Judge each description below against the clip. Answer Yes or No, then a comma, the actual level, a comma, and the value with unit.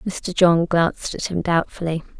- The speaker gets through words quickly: No, average, 165 wpm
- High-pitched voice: No, medium, 170 Hz